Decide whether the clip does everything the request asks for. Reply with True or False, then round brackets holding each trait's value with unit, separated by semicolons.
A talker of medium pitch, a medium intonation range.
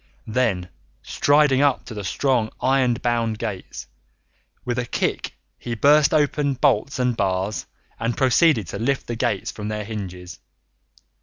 False (120 Hz; 4.3 semitones)